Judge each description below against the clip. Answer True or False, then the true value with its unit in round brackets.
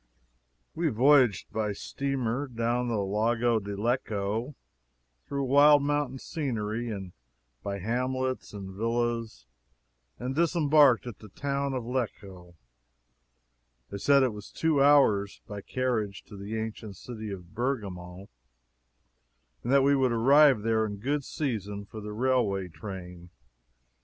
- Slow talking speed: True (130 wpm)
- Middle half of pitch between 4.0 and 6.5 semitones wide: True (4.7 semitones)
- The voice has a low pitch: True (115 Hz)